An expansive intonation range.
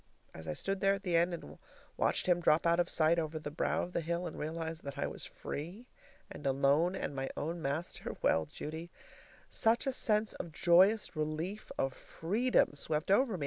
No: average, 3.7 semitones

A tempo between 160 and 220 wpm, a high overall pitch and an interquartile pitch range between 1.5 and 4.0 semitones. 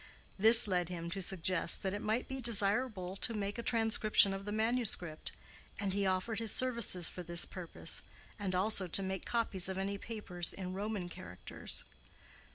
Yes: average, 170 wpm; high, 195 Hz; average, 3.3 semitones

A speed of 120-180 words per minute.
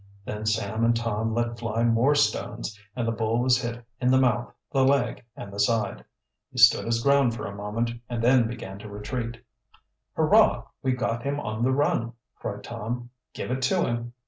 No: average, 195 wpm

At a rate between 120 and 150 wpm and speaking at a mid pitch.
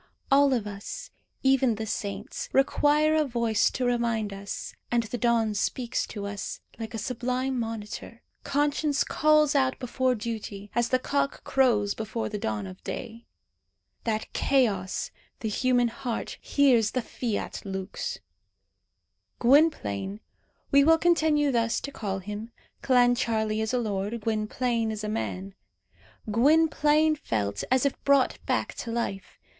No: average, 140 wpm; high, 235 Hz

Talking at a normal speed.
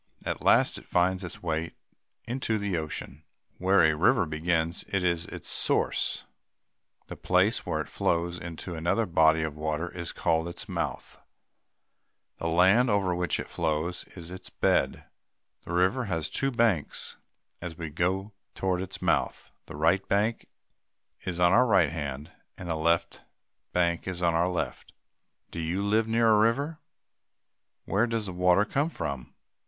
Yes: average, 160 wpm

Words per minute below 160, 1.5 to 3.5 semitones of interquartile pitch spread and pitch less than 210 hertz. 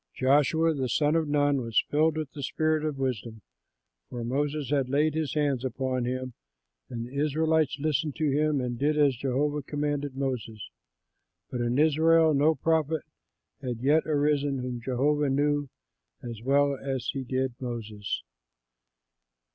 Yes: average, 150 wpm; average, 2.8 semitones; medium, 140 Hz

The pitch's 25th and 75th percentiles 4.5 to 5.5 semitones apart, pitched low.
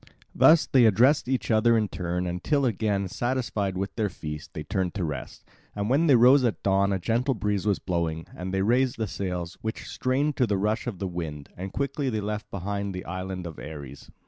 Yes: average, 4.8 semitones; low, 100 Hz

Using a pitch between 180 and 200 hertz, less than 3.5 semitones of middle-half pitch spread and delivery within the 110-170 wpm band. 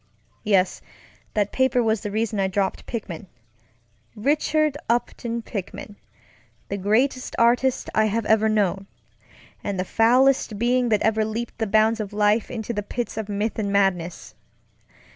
No: high, 220 Hz; average, 2.7 semitones; average, 145 wpm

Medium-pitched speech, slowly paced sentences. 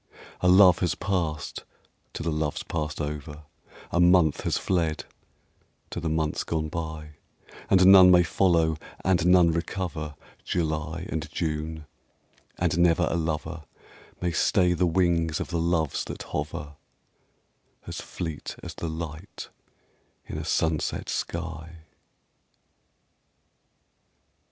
No: very low, 80 Hz; slow, 120 wpm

